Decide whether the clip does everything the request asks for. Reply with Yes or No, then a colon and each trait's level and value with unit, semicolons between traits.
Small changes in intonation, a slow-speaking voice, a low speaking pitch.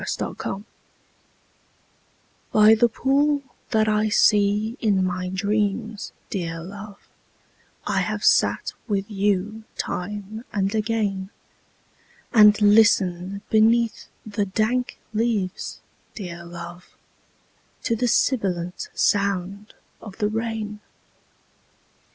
No: narrow, 2.3 semitones; slow, 100 wpm; high, 210 Hz